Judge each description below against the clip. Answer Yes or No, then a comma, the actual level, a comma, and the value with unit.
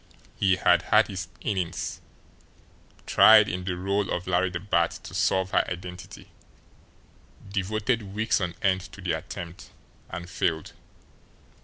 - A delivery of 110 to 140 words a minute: Yes, slow, 135 wpm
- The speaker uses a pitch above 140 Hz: No, very low, 95 Hz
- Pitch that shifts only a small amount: Yes, narrow, 1.9 semitones